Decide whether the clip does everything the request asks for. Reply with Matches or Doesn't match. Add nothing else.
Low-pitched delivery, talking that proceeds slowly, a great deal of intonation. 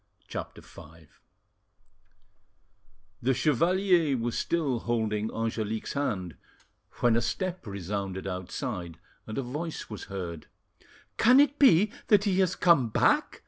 Matches